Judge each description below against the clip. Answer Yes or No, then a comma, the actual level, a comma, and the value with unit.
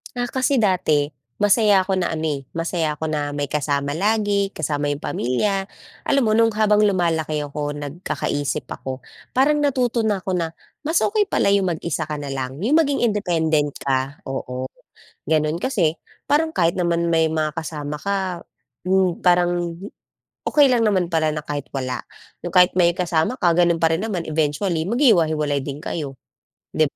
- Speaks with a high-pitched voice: No, medium, 170 Hz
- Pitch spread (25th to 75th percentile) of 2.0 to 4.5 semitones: No, average, 5.1 semitones